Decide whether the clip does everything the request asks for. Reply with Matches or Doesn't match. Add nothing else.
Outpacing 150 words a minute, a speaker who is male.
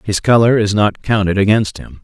Matches